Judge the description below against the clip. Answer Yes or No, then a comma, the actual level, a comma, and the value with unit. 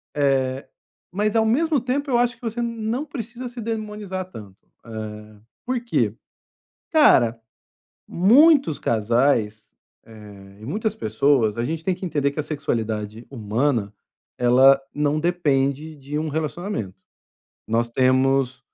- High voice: No, medium, 145 Hz